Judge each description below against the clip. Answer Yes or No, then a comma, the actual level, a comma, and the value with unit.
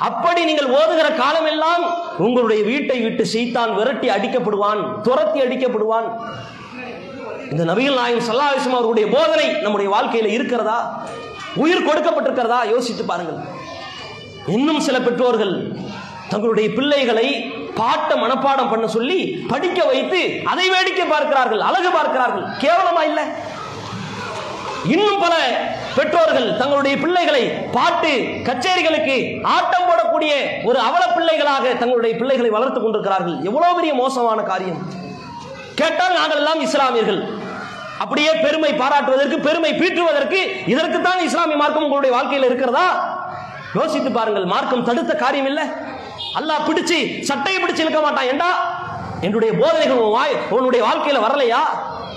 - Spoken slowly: Yes, slow, 115 wpm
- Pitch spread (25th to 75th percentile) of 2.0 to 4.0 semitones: No, wide, 5.6 semitones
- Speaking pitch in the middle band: No, very high, 280 Hz